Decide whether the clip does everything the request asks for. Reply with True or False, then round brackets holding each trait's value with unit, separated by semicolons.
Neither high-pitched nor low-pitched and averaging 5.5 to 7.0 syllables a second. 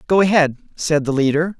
True (160 Hz; 5.6 syllables/s)